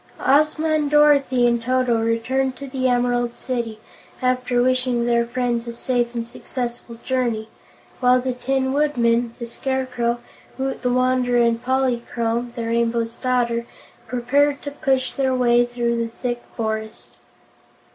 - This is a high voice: Yes, high, 245 Hz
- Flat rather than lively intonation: Yes, narrow, 1.7 semitones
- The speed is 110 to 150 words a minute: Yes, average, 140 wpm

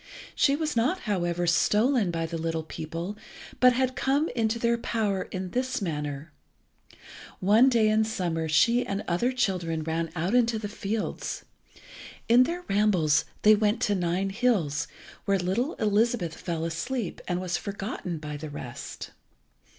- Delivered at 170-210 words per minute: No, average, 155 wpm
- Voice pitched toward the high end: Yes, high, 200 Hz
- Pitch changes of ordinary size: No, wide, 5.9 semitones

